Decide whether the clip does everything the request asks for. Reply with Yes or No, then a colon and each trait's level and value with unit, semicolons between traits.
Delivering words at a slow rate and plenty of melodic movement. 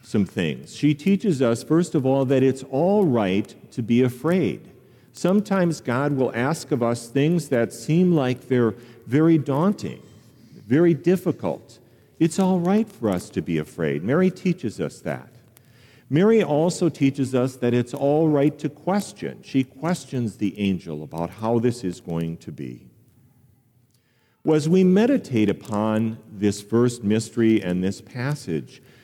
No: average, 155 wpm; wide, 5.8 semitones